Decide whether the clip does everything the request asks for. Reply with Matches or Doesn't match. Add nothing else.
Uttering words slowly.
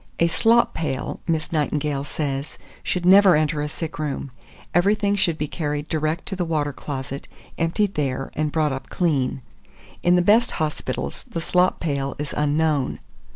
Doesn't match